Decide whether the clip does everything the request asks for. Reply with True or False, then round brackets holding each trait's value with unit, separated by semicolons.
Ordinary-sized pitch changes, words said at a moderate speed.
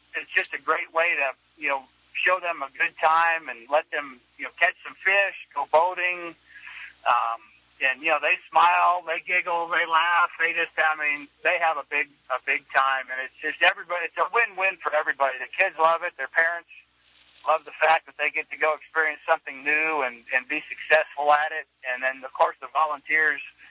False (3.5 semitones; 210 wpm)